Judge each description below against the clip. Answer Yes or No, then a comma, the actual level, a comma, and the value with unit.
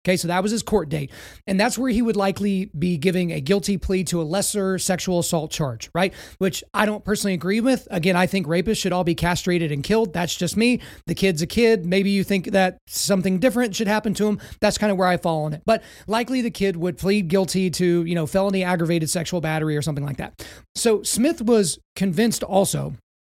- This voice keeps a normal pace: No, fast, 230 wpm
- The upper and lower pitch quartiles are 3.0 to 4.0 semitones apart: Yes, average, 3.3 semitones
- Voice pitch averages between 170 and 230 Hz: Yes, high, 190 Hz